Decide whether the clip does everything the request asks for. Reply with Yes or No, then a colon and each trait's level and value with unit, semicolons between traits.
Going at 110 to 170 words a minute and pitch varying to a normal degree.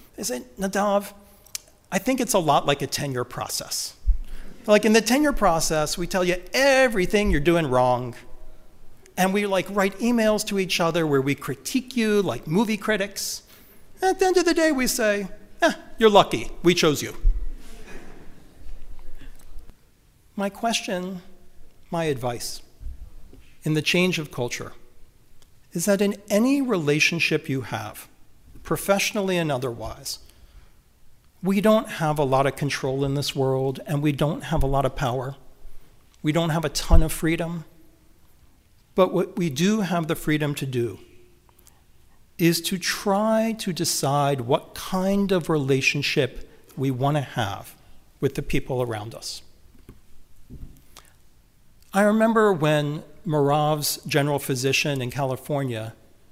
No: average, 140 wpm; wide, 6.7 semitones